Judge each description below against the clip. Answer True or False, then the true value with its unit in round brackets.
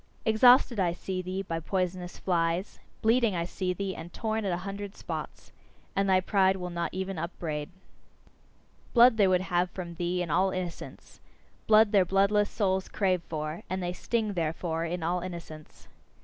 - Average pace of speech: True (170 wpm)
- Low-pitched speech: False (185 Hz)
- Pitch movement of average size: False (2.3 semitones)